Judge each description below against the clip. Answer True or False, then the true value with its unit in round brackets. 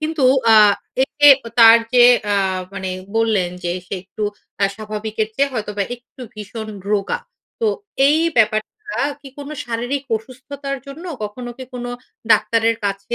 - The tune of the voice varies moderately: True (4.0 semitones)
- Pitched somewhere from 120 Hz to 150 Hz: False (230 Hz)